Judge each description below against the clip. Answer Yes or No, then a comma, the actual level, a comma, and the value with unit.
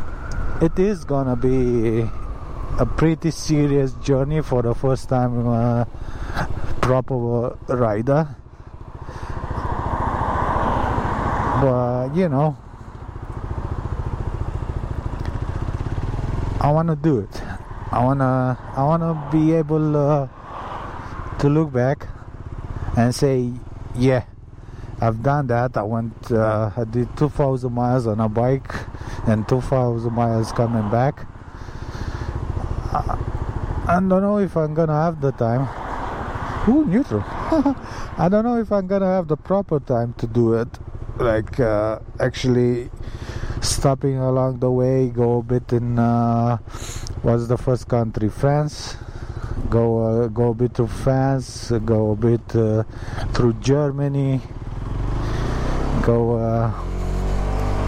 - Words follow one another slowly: Yes, slow, 115 wpm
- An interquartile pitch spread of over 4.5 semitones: No, average, 2.9 semitones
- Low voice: Yes, low, 120 Hz